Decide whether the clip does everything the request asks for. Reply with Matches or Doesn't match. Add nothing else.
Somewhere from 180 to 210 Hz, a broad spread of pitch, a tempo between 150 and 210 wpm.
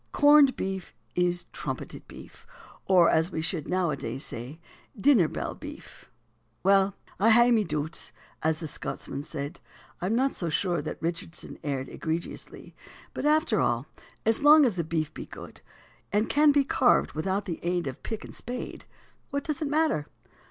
Matches